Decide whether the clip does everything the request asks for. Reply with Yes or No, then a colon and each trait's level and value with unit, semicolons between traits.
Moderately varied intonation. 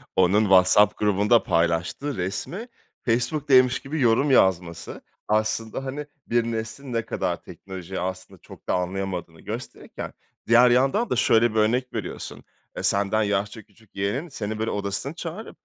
Yes: average, 4.3 semitones